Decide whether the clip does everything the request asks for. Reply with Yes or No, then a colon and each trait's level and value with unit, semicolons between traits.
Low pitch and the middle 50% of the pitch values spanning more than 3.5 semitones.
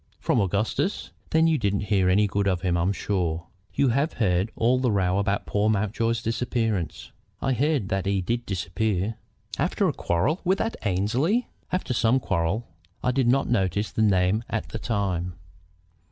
Yes: low, 105 Hz; average, 4.3 semitones